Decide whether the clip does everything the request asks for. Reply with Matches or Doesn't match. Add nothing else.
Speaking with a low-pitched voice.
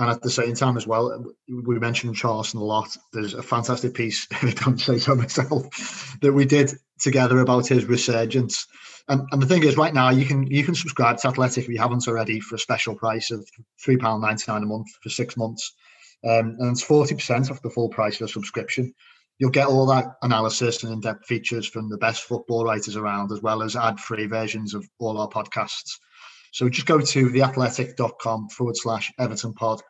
Matches